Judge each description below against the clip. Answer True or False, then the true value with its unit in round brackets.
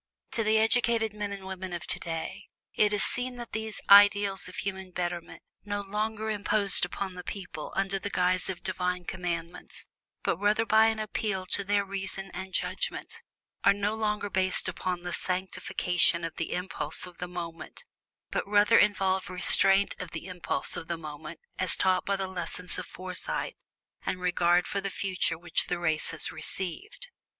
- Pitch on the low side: False (190 Hz)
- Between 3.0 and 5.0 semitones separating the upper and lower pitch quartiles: False (2.4 semitones)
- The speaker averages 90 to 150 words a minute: False (175 wpm)